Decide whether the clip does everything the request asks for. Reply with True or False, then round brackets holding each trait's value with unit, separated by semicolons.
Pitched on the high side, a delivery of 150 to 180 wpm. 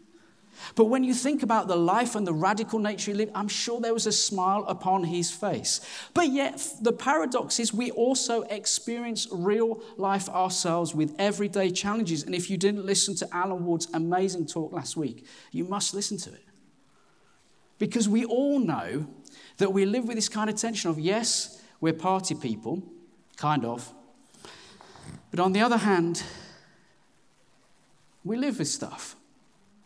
True (200 Hz; 165 wpm)